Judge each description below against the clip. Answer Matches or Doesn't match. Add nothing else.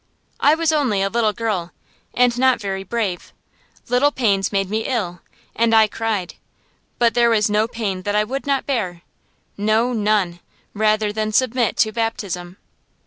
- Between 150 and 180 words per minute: Matches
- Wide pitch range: Doesn't match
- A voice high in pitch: Matches